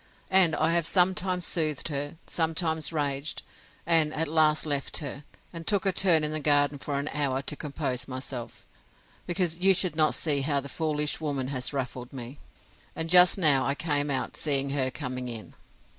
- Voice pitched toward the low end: No, medium, 150 Hz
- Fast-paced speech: No, average, 180 wpm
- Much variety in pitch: No, average, 2.9 semitones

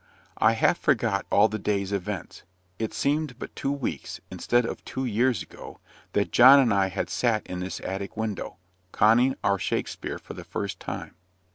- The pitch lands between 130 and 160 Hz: No, low, 110 Hz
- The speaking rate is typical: Yes, average, 175 wpm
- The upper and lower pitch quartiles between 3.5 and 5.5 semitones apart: Yes, average, 4.1 semitones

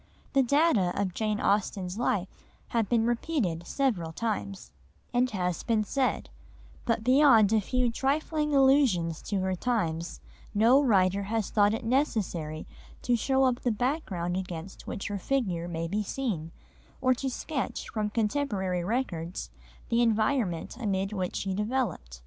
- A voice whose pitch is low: No, high, 215 Hz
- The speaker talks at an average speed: Yes, average, 145 wpm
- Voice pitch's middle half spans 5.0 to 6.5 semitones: Yes, wide, 5.4 semitones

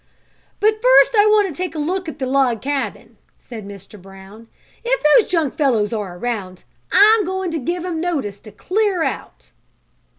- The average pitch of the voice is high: Yes, very high, 300 Hz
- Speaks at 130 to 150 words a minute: No, average, 175 wpm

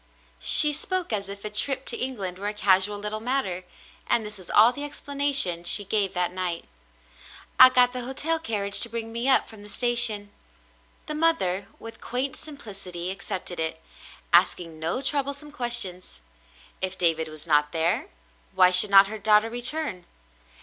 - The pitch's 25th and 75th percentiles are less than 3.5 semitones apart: No, wide, 5.6 semitones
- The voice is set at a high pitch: Yes, high, 210 Hz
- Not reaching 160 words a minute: No, average, 170 wpm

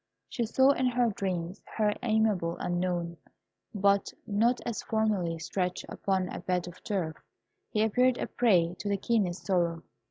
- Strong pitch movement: No, average, 3.9 semitones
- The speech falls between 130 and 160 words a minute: Yes, average, 155 wpm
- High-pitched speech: Yes, high, 195 Hz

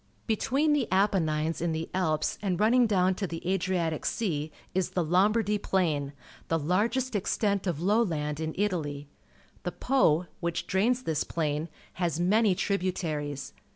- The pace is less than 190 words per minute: Yes, average, 155 wpm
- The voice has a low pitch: No, medium, 180 Hz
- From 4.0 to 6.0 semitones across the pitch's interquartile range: Yes, average, 4.5 semitones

